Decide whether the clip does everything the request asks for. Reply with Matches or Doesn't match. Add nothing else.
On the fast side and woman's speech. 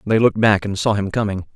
Doesn't match